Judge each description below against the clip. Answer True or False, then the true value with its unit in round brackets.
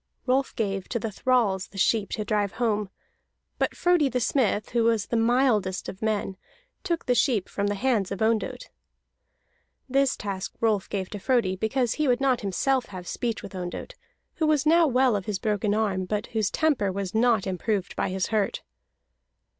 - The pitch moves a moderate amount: True (4.2 semitones)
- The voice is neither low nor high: False (220 Hz)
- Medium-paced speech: True (185 wpm)